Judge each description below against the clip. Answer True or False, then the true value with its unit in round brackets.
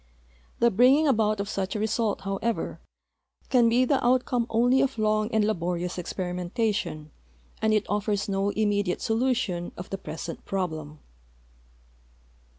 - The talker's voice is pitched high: True (210 Hz)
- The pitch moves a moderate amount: True (3.7 semitones)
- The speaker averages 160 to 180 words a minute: False (145 wpm)